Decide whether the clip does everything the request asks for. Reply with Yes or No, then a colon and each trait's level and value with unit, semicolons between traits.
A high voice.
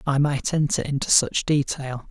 No: medium, 140 Hz